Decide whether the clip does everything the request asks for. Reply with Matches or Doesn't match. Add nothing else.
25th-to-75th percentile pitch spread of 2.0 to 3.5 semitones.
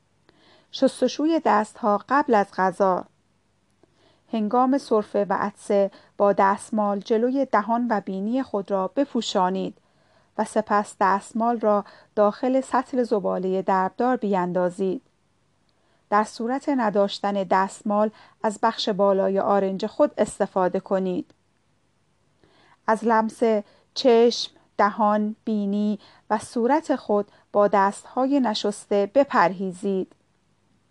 Matches